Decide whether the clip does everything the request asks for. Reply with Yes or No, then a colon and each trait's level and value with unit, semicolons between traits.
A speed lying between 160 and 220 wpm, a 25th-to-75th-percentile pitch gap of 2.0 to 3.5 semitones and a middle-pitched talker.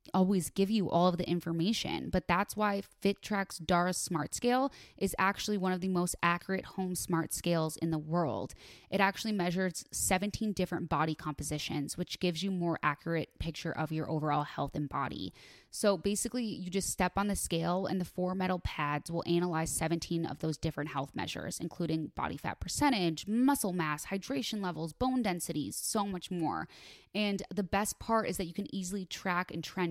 Yes: average, 185 wpm; average, 3.1 semitones; medium, 180 Hz